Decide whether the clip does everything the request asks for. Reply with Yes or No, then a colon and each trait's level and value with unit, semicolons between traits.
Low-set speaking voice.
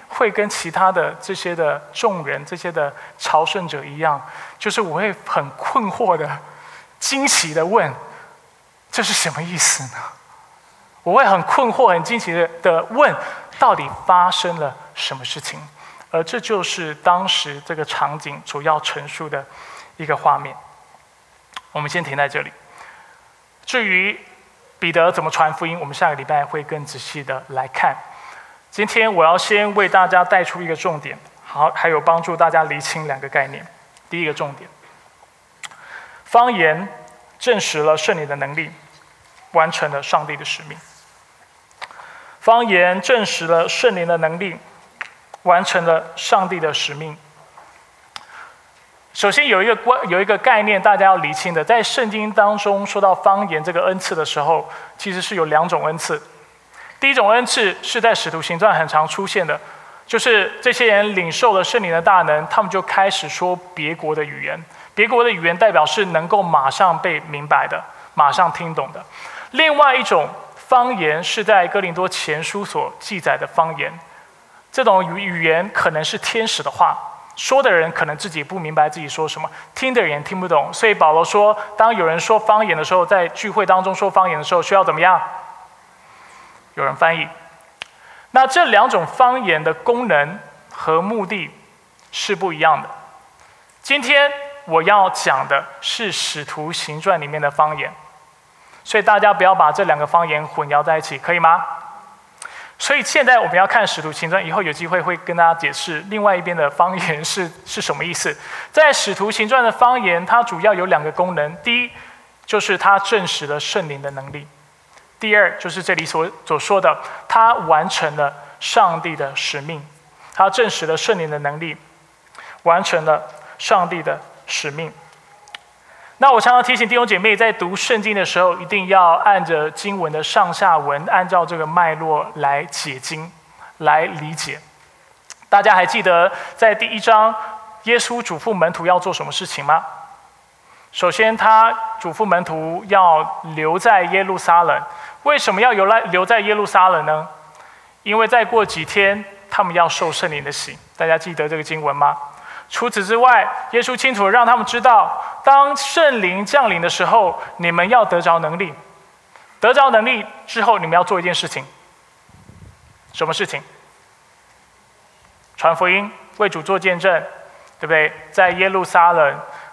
No: medium, 180 Hz